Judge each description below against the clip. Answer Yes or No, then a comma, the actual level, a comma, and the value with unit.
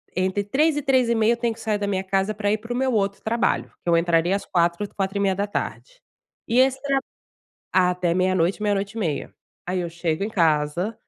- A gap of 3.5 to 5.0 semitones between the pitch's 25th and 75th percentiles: Yes, average, 4.1 semitones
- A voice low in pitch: No, high, 200 Hz